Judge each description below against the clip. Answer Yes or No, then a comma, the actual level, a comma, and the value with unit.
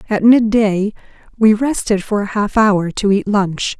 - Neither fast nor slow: Yes, average, 190 wpm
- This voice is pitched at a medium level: No, high, 210 Hz